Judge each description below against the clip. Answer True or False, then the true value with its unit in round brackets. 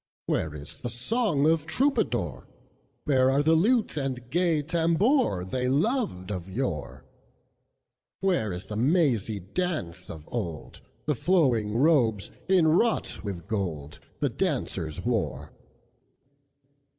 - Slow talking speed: True (100 wpm)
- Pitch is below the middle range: True (130 Hz)